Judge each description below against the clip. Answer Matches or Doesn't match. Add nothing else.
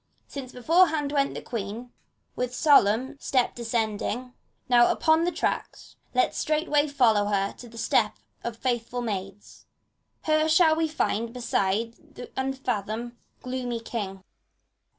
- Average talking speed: Doesn't match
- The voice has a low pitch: Doesn't match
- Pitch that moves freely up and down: Doesn't match